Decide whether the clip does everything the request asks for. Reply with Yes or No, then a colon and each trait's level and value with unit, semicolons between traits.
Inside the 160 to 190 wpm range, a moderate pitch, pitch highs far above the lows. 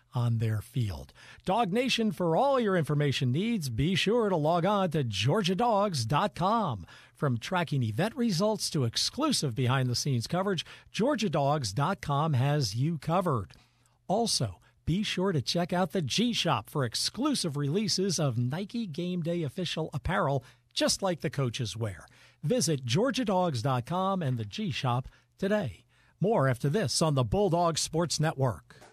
No: average, 145 wpm; medium, 160 Hz; wide, 7.1 semitones